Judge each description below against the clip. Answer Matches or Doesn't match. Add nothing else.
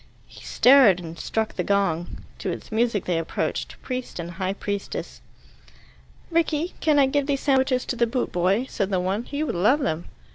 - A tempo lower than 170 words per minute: Doesn't match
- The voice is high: Matches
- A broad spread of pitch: Matches